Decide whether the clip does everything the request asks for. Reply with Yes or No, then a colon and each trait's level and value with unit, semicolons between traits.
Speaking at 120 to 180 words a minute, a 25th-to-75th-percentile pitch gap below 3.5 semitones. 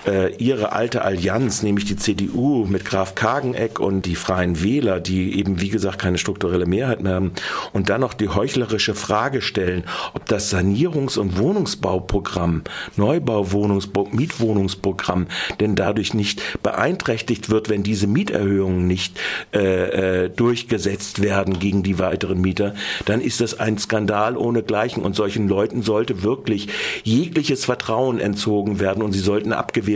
Yes: average, 145 wpm; narrow, 2.5 semitones